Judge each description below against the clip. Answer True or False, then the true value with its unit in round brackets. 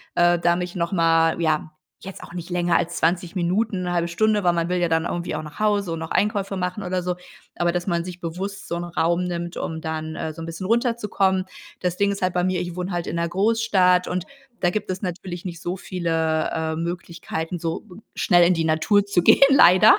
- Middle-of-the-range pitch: True (175 Hz)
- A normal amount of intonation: False (1.8 semitones)